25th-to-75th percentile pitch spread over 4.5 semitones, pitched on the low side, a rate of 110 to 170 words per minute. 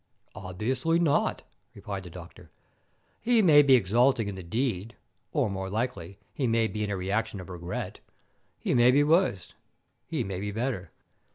Yes: wide, 5.5 semitones; low, 110 Hz; average, 165 wpm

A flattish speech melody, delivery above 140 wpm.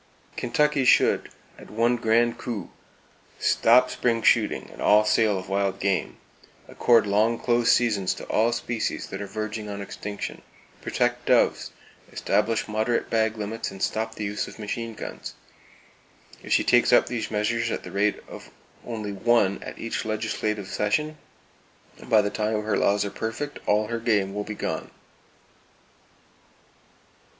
Yes: narrow, 2.1 semitones; average, 150 wpm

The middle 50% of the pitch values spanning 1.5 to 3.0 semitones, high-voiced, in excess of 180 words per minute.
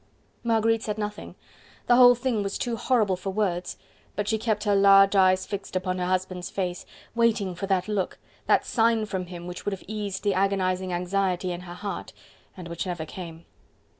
Yes: average, 2.7 semitones; high, 195 Hz; average, 190 wpm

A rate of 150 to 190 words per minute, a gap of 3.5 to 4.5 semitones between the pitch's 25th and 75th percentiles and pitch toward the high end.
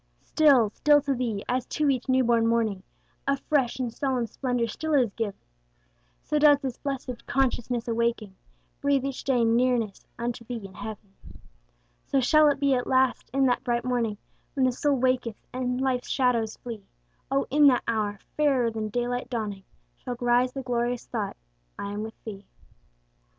No: average, 170 wpm; average, 2.7 semitones; high, 245 Hz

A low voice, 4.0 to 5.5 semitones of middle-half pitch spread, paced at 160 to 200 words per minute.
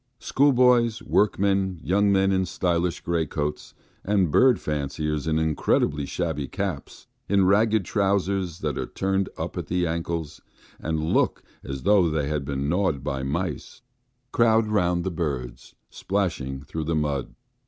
No: very low, 85 Hz; average, 4.7 semitones; average, 145 wpm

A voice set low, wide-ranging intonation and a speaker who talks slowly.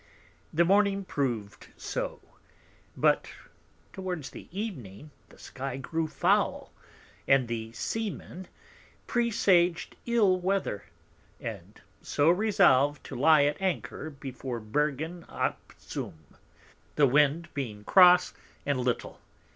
No: medium, 155 Hz; wide, 5.9 semitones; slow, 105 wpm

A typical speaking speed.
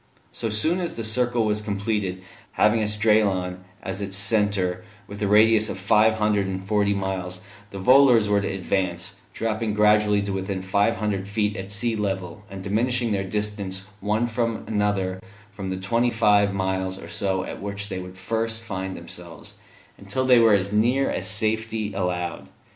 Yes: average, 170 wpm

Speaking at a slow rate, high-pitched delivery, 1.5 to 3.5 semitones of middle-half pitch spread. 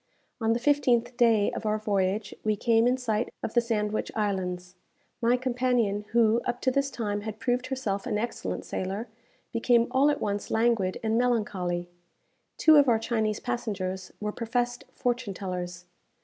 No: average, 165 wpm; high, 225 Hz; average, 3.1 semitones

